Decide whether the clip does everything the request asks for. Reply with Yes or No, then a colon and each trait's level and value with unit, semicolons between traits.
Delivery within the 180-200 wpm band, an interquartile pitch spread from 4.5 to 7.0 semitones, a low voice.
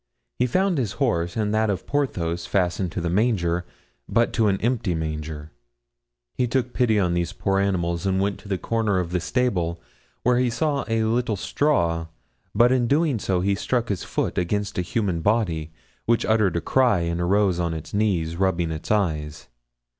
Yes: average, 185 wpm; average, 5.2 semitones; low, 100 Hz